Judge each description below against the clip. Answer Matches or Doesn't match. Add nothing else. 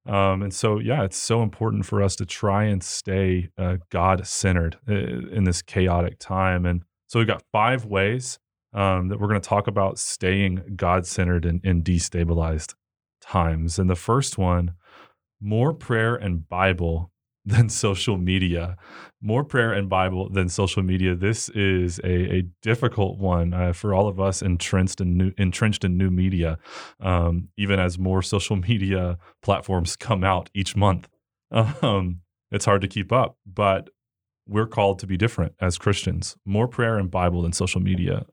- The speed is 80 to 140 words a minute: Doesn't match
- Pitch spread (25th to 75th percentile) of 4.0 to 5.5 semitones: Doesn't match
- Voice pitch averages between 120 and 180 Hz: Doesn't match